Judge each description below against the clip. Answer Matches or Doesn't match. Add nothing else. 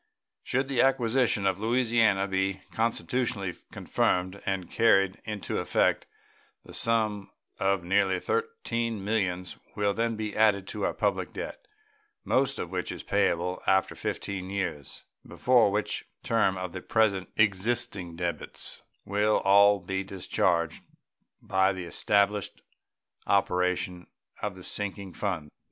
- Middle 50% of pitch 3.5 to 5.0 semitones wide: Doesn't match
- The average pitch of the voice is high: Doesn't match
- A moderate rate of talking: Doesn't match